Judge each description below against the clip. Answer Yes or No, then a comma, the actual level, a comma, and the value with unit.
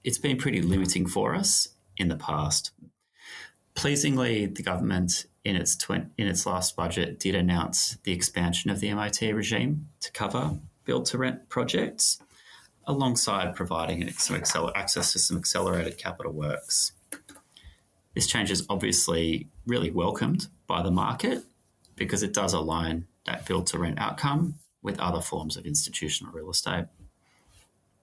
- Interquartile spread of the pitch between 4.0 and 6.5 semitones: Yes, wide, 5.5 semitones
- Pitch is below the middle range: Yes, very low, 95 Hz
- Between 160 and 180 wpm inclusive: No, average, 145 wpm